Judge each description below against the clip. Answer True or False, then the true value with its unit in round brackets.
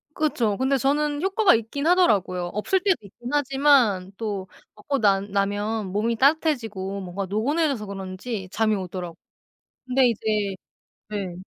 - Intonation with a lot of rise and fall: True (5.9 semitones)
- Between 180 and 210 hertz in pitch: False (220 Hz)